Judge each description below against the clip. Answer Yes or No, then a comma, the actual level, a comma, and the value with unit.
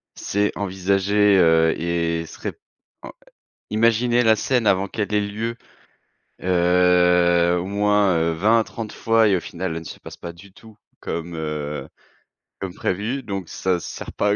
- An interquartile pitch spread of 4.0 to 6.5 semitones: No, average, 3.3 semitones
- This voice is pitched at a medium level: No, very low, 95 Hz